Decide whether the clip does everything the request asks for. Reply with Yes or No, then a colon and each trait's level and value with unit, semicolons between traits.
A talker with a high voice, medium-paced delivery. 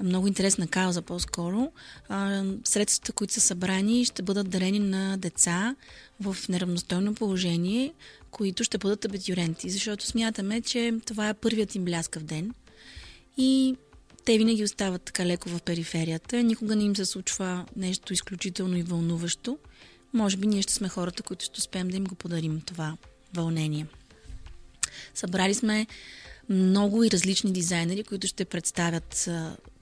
Yes: high, 195 Hz; average, 145 wpm